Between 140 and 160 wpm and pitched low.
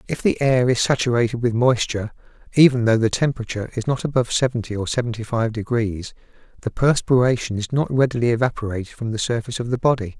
No: average, 180 wpm; low, 120 Hz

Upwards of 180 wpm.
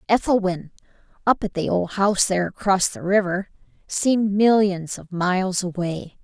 No: average, 145 wpm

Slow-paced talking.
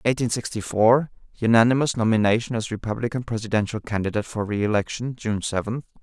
Yes: slow, 120 wpm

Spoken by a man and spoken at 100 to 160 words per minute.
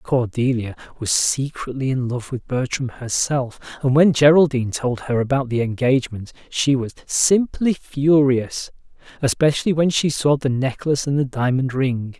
Yes: male; average, 150 wpm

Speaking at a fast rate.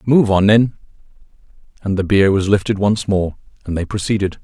No: average, 175 wpm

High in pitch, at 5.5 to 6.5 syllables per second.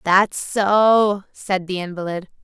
No: high, 195 Hz; 3.3 syllables/s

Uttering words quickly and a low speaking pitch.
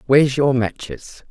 No: average, 140 wpm; low, 125 Hz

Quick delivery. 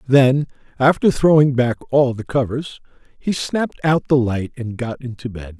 No: average, 170 wpm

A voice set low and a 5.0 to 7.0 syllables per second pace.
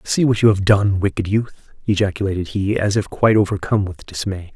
Yes: low, 100 Hz; 5.8 syllables/s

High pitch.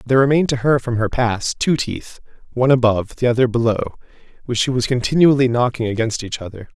No: low, 120 Hz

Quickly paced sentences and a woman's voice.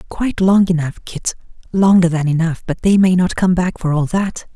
No: fast, 210 wpm; male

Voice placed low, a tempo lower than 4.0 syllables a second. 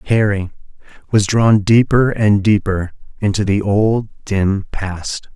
Yes: low, 105 Hz; 3.7 syllables/s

